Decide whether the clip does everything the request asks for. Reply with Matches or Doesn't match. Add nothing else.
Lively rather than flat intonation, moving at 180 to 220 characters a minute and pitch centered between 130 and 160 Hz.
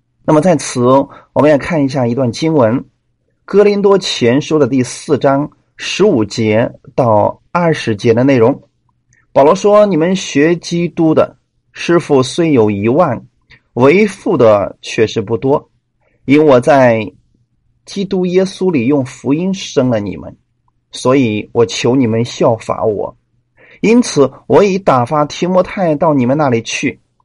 Matches